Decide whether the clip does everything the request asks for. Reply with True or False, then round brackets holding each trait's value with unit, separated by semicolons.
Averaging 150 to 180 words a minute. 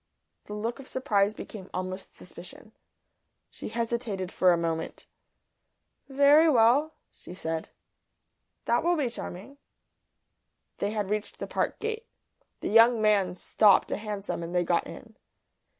False (135 wpm)